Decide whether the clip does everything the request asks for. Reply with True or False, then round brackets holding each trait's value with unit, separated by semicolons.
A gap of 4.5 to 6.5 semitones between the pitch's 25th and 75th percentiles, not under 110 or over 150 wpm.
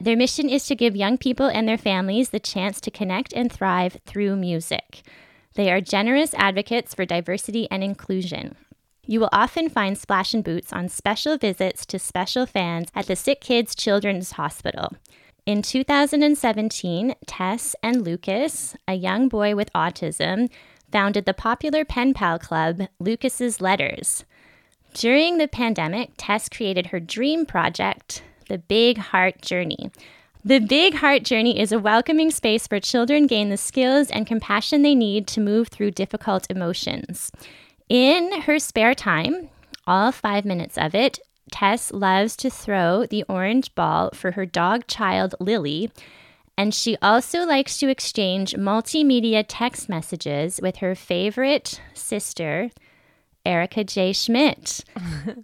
True (4.9 semitones; 145 wpm)